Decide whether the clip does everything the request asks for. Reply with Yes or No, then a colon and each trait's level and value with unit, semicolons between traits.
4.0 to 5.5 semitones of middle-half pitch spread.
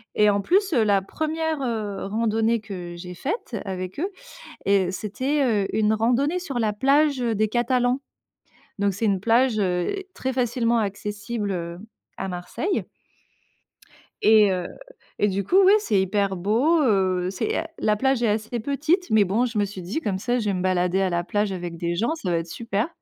Yes: average, 4.6 semitones